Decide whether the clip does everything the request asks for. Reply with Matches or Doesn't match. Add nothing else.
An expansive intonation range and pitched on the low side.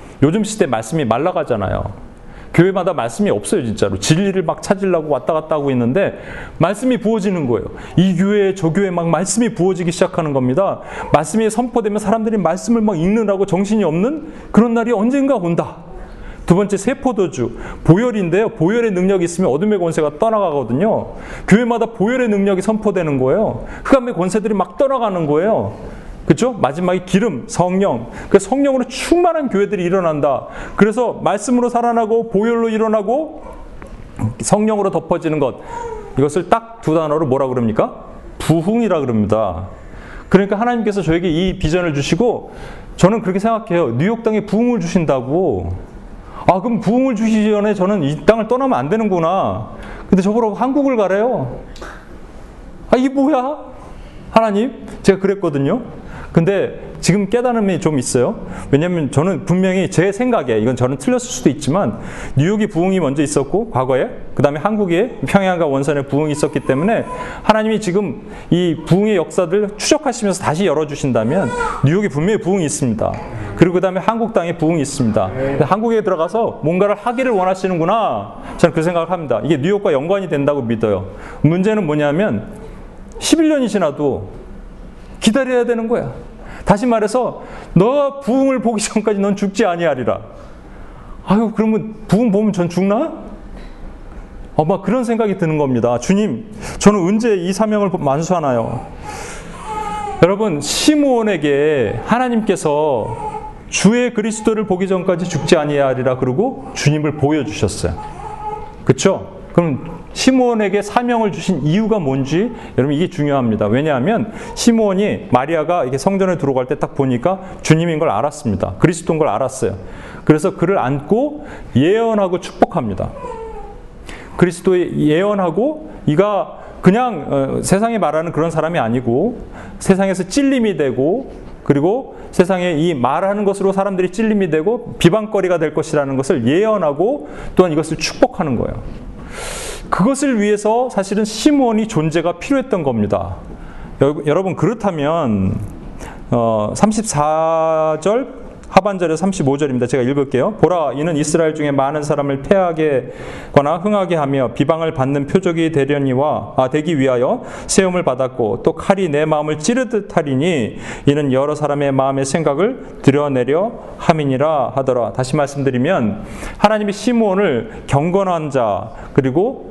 Doesn't match